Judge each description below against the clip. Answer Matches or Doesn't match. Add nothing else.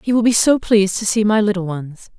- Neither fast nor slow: Doesn't match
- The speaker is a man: Doesn't match